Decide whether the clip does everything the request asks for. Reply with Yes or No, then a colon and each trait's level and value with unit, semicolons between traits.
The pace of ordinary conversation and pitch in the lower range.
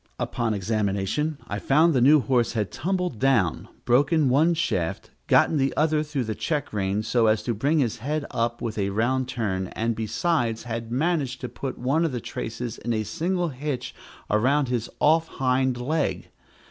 Yes: average, 180 wpm; low, 125 Hz